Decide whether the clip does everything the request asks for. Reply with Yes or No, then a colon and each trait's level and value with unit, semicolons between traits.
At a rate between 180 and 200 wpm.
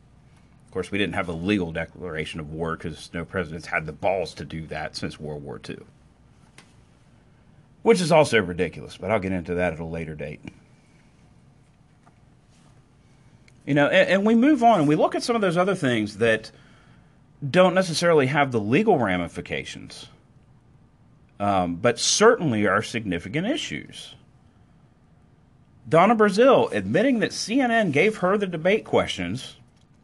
No: average, 150 wpm